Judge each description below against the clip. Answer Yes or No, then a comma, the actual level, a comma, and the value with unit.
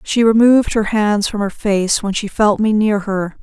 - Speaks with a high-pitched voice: Yes, high, 210 Hz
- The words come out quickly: Yes, fast, 230 wpm